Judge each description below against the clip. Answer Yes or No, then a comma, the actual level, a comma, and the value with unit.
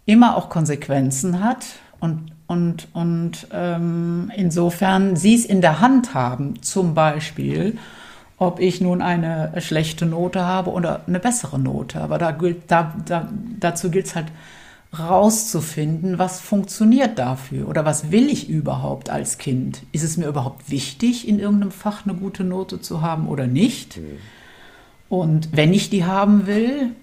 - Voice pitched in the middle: Yes, medium, 175 Hz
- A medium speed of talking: Yes, average, 155 wpm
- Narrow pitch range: No, average, 3.7 semitones